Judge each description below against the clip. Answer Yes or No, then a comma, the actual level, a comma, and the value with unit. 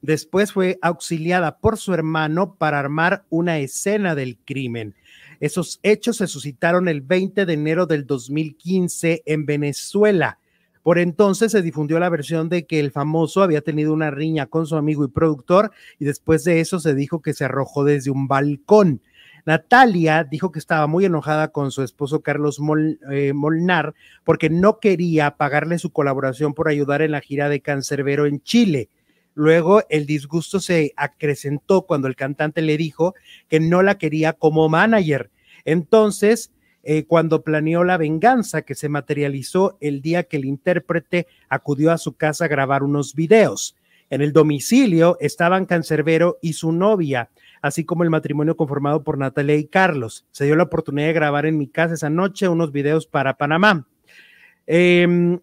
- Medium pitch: Yes, medium, 155 Hz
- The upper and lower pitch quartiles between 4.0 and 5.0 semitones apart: No, average, 3.2 semitones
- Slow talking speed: No, average, 165 wpm